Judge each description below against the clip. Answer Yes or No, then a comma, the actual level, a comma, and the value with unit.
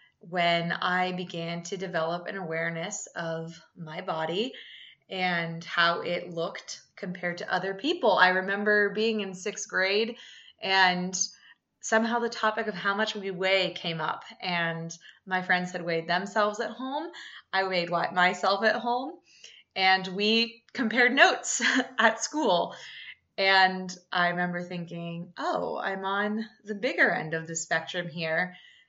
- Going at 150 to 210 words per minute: No, average, 140 wpm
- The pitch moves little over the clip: No, average, 3.7 semitones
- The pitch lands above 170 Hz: Yes, medium, 185 Hz